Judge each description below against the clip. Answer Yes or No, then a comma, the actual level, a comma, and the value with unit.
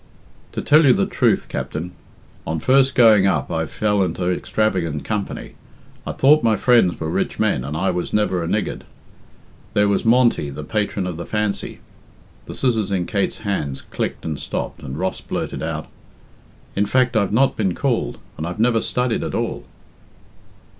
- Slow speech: No, average, 175 wpm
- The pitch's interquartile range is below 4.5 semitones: No, average, 4.8 semitones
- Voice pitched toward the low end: Yes, low, 100 Hz